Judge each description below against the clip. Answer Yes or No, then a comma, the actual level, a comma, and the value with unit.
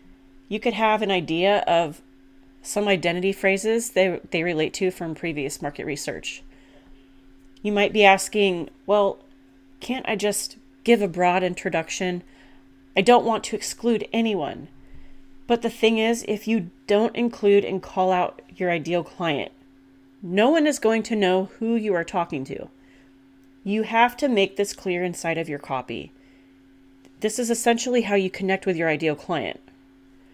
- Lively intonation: Yes, wide, 8.1 semitones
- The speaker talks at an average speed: Yes, average, 160 wpm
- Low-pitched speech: No, medium, 185 Hz